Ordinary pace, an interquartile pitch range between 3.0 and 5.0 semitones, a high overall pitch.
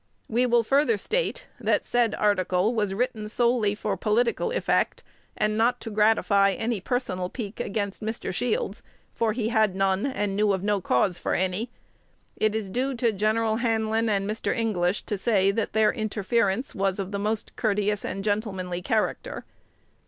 No: average, 165 wpm; narrow, 2.6 semitones; high, 215 Hz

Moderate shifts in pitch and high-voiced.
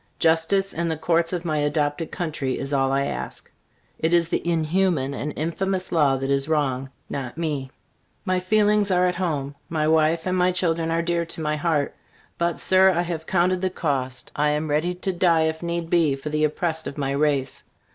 No: average, 3.1 semitones; medium, 160 Hz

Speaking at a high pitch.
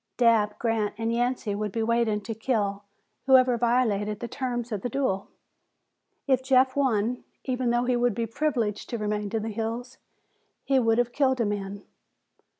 Yes: high, 230 Hz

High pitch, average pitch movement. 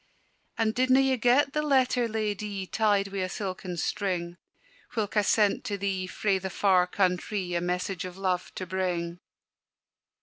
Yes: high, 195 Hz; average, 3.1 semitones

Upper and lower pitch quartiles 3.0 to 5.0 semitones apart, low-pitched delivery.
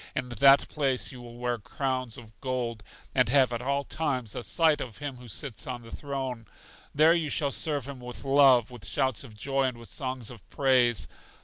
No: narrow, 2.6 semitones; low, 130 Hz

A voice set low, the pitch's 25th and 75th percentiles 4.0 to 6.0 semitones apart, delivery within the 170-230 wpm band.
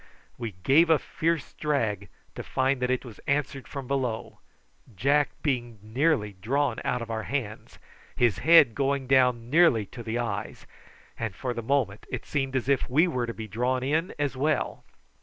No: low, 130 Hz; average, 3.5 semitones; average, 175 wpm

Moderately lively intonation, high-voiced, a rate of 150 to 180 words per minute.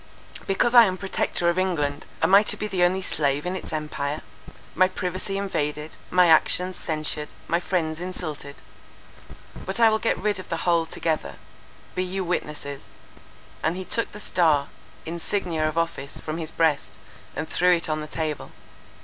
No: average, 3.3 semitones; medium, 170 Hz; average, 165 wpm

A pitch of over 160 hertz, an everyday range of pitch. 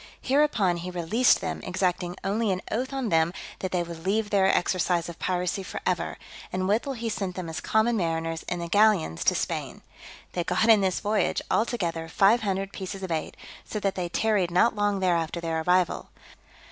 Yes: medium, 185 Hz; average, 3.6 semitones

